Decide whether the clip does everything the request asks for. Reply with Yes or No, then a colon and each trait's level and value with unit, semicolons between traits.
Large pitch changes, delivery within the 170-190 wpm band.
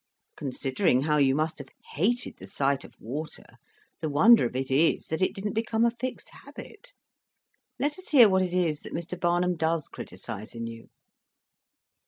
Yes: wide, 7.1 semitones; average, 175 wpm